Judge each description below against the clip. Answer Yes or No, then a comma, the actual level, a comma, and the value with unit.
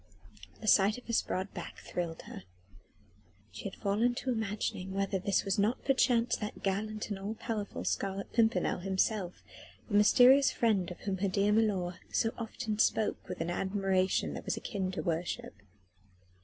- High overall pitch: Yes, high, 200 Hz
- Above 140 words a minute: Yes, average, 165 wpm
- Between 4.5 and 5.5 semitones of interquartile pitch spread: No, average, 2.7 semitones